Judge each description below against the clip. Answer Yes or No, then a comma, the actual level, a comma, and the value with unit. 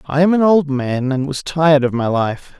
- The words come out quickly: Yes, fast, 255 wpm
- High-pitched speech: No, medium, 145 Hz